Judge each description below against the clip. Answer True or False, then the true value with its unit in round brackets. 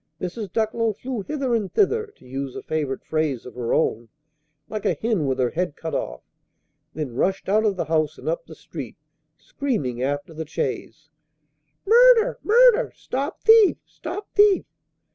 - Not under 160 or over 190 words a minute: True (165 wpm)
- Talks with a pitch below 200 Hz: True (190 Hz)